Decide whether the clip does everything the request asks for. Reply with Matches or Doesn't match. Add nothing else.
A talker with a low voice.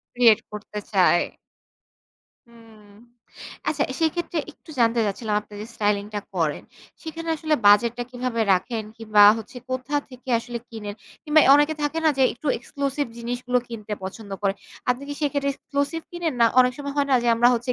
Doesn't match